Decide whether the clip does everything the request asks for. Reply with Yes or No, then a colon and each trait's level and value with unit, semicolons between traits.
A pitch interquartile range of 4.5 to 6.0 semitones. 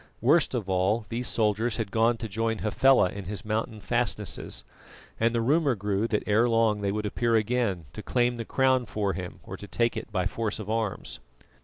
No: narrow, 2.4 semitones